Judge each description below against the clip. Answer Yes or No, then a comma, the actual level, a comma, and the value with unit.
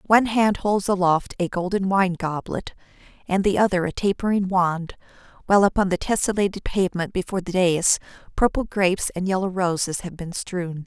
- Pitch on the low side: No, medium, 185 Hz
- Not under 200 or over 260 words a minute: No, average, 165 wpm